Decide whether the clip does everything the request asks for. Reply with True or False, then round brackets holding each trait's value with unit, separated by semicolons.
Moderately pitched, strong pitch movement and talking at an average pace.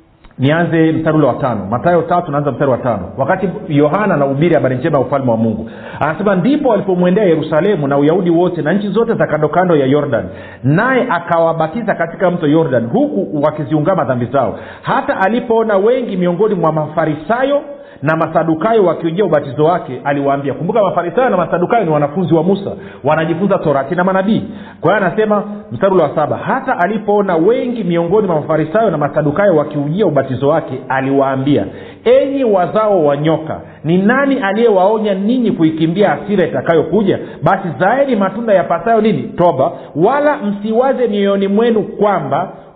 False (175 Hz; 5.7 semitones; 150 wpm)